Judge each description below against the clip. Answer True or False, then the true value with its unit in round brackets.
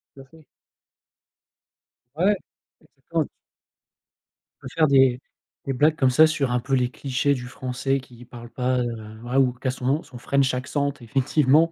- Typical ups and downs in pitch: False (2.3 semitones)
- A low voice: True (130 Hz)